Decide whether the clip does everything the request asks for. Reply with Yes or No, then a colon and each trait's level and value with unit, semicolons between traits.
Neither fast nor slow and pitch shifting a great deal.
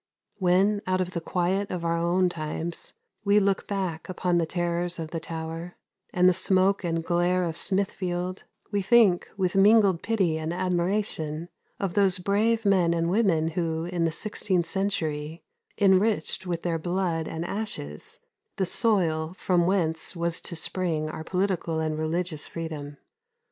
No: average, 155 wpm; average, 2.7 semitones